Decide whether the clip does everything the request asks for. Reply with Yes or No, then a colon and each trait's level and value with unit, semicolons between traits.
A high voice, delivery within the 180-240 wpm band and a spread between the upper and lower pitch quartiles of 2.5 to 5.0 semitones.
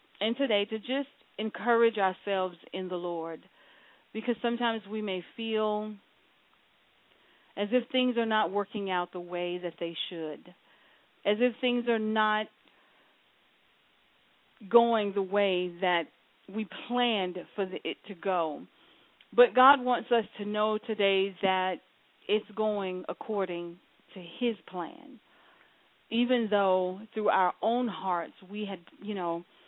No: high, 205 Hz; slow, 135 wpm; average, 3.7 semitones